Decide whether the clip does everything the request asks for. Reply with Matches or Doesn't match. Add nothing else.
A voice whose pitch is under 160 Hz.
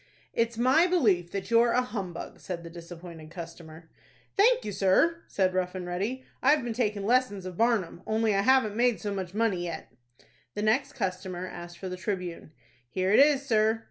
Doesn't match